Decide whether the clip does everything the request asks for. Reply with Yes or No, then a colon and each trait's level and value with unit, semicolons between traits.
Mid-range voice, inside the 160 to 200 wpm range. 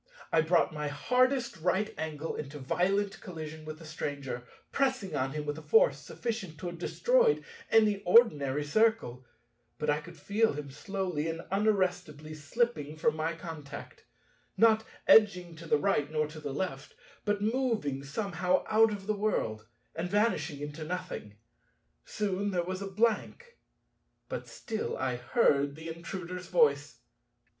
No: medium, 175 Hz; average, 150 wpm